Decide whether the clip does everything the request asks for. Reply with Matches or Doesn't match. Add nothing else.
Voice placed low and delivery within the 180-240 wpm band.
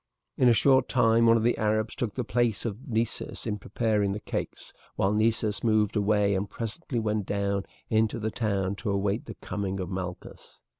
Matches